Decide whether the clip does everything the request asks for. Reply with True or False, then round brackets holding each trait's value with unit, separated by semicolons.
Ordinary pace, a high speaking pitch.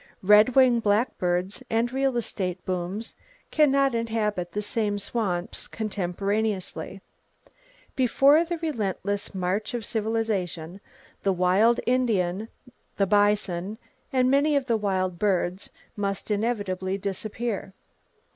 False (110 wpm; 210 Hz)